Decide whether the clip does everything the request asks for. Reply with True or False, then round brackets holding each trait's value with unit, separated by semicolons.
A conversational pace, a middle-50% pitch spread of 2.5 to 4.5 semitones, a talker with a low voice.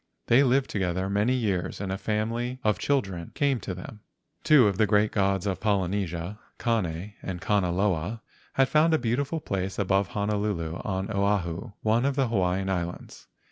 True (165 wpm; 3.7 semitones; 100 Hz)